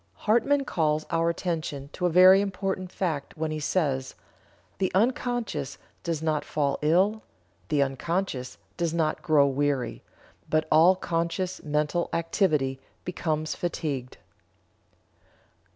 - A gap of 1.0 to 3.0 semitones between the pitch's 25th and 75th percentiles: No, average, 3.7 semitones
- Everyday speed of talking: No, slow, 120 wpm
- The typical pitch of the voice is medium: Yes, medium, 160 Hz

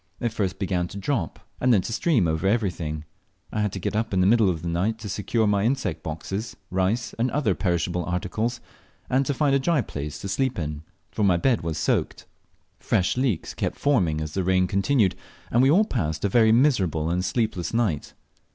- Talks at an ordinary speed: No, fast, 210 wpm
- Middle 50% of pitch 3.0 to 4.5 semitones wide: No, average, 5.3 semitones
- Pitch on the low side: Yes, low, 100 Hz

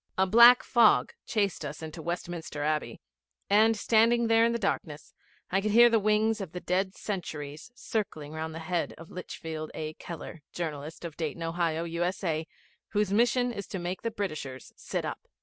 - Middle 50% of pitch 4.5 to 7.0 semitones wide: Yes, average, 5.1 semitones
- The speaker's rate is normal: Yes, average, 180 wpm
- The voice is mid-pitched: Yes, medium, 180 Hz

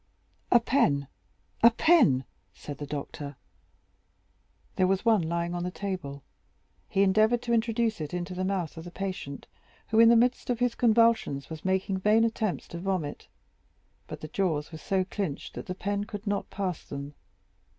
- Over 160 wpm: Yes, average, 170 wpm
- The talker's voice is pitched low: No, high, 190 Hz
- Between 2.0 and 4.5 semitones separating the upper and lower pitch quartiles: No, wide, 5.5 semitones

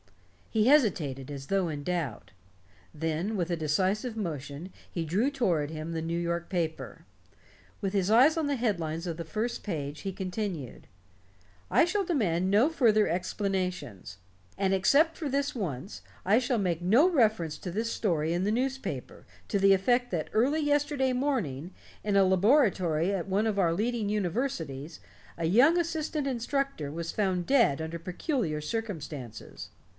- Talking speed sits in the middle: Yes, average, 160 wpm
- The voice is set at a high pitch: Yes, high, 195 Hz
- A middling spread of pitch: No, wide, 6.8 semitones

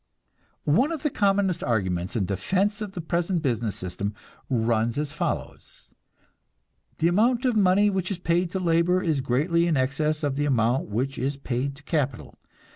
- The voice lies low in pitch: No, medium, 150 Hz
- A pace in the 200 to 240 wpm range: No, average, 170 wpm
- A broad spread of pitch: Yes, wide, 6.8 semitones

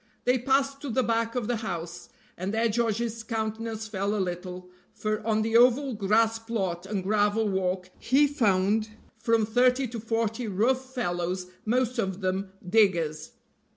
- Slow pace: No, average, 155 wpm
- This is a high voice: Yes, high, 220 Hz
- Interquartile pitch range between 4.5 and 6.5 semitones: No, average, 3.5 semitones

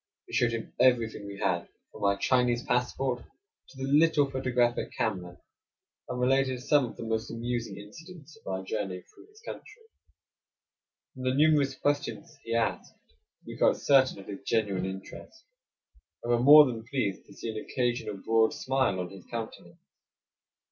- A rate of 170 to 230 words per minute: No, average, 160 wpm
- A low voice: Yes, low, 120 Hz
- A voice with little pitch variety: No, average, 4.3 semitones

